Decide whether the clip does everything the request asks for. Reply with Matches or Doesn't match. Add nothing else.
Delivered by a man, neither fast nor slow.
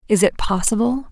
Doesn't match